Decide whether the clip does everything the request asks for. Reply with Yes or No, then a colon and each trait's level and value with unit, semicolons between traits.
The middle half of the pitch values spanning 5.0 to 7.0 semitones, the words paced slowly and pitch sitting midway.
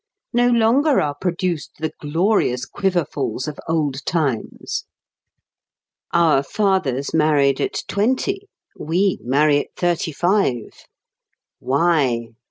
Yes: wide, 5.4 semitones; slow, 100 wpm; medium, 160 Hz